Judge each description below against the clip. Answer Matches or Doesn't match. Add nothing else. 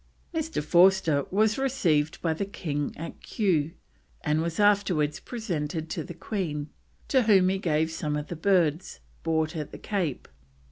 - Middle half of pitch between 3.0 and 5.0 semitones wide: Matches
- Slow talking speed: Doesn't match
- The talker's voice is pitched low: Doesn't match